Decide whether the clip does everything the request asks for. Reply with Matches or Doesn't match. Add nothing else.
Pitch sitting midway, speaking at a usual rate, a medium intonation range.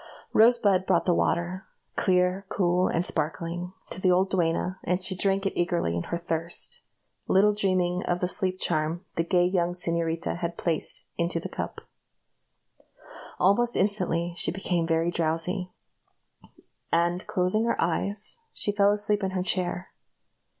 Doesn't match